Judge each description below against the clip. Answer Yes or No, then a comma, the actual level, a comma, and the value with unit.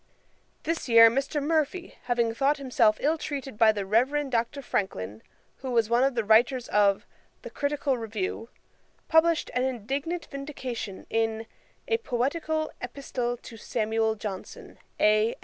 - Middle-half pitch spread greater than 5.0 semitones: No, average, 4.2 semitones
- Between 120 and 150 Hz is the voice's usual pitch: No, high, 245 Hz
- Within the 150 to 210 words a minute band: No, average, 140 wpm